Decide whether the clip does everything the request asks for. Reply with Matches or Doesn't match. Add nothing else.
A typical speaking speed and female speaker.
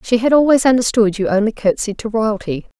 Matches